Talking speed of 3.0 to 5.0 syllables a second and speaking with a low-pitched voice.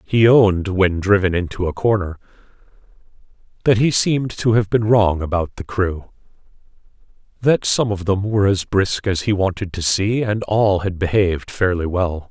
Yes: 4.9 syllables/s; low, 100 Hz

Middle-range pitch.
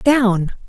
No: high, 225 Hz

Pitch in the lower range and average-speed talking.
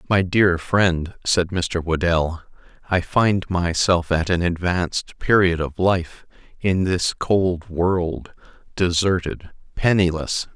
No: very low, 90 Hz; slow, 120 wpm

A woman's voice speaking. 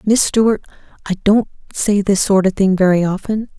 Yes: female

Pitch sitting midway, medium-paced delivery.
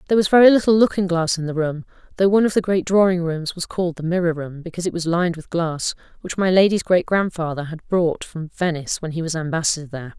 No: medium, 175 Hz; fast, 240 wpm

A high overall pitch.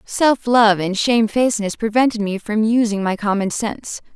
Yes: high, 220 Hz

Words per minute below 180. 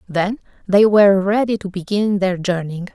Yes: average, 165 wpm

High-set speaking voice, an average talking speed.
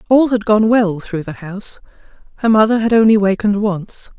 Yes: high, 210 Hz; average, 185 wpm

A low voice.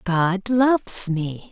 No: high, 195 Hz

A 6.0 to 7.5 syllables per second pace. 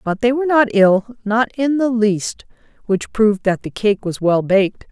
No: 4.7 syllables/s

